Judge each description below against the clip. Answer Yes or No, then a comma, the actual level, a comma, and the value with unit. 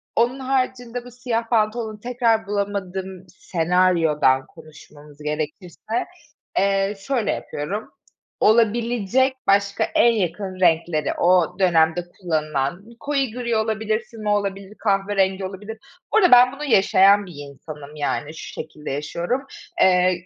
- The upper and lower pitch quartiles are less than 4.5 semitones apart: No, average, 4.8 semitones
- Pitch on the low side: No, high, 195 Hz